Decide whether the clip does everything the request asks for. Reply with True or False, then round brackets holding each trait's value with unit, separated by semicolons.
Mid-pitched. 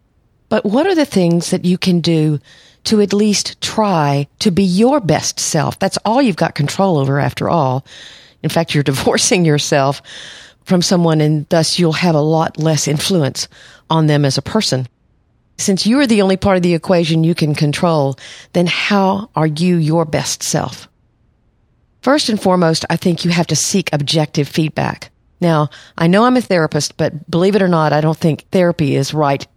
True (165 Hz)